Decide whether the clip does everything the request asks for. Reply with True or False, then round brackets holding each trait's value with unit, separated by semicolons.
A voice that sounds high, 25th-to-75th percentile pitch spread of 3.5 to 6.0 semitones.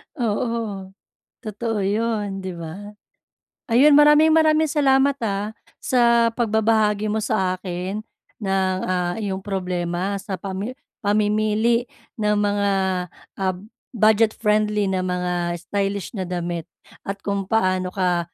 False (205 Hz; 3.1 semitones)